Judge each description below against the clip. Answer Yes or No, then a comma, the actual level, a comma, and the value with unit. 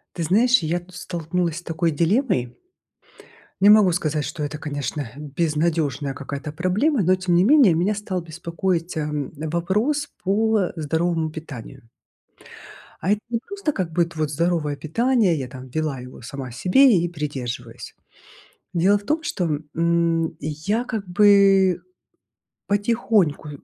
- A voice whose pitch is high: No, medium, 170 Hz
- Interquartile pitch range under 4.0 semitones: No, average, 4.7 semitones